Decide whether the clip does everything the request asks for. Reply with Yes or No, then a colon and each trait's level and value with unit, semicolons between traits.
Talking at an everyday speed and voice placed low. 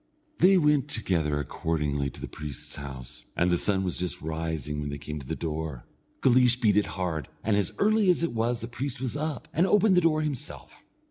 No: fast, 210 wpm; low, 100 Hz